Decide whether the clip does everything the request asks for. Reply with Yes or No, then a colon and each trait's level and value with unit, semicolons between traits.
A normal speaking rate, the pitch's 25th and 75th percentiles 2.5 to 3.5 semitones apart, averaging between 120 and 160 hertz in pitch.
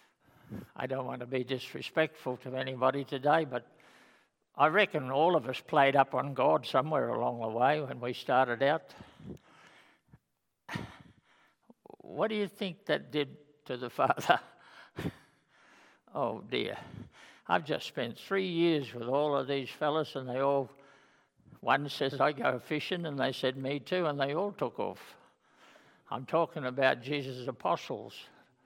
Yes: average, 150 wpm; average, 2.9 semitones; medium, 140 Hz